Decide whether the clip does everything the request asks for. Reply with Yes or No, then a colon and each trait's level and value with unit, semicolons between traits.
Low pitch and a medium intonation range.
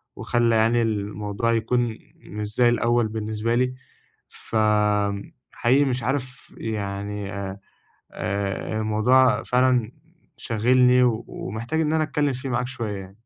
Yes: low, 115 Hz; average, 3.1 semitones